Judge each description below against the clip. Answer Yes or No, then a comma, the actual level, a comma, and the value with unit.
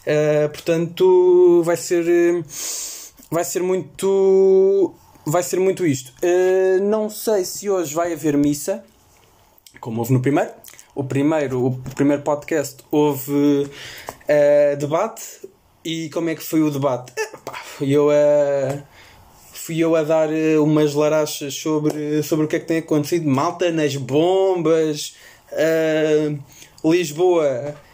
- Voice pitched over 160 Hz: No, medium, 155 Hz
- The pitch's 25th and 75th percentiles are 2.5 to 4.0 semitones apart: Yes, average, 3.2 semitones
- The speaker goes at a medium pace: Yes, average, 135 wpm